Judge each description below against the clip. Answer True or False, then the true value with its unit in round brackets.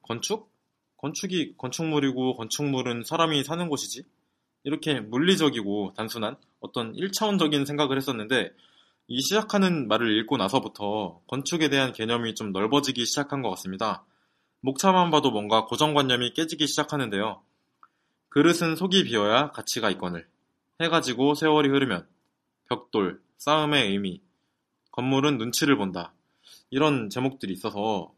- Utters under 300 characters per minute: False (315 characters per minute)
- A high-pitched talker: False (135 Hz)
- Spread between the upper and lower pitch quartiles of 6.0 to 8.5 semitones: False (5.5 semitones)